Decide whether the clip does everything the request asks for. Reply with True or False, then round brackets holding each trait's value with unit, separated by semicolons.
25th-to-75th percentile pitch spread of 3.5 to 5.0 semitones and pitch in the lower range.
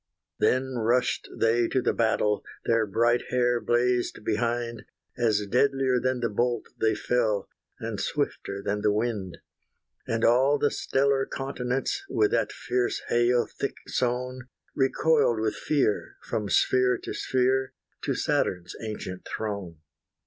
False (2.9 semitones; 120 Hz)